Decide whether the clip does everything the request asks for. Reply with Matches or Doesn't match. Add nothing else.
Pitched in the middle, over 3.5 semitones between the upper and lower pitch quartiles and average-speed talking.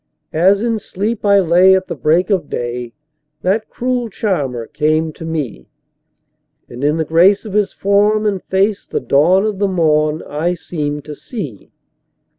Matches